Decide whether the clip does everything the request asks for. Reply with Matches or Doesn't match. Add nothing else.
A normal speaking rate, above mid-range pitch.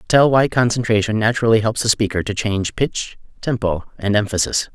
Doesn't match